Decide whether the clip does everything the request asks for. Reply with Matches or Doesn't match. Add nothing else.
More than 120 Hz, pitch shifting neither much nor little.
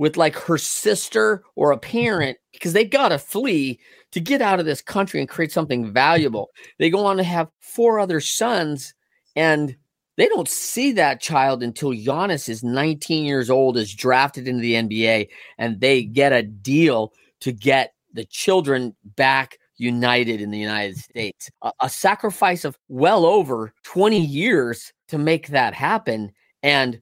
Doesn't match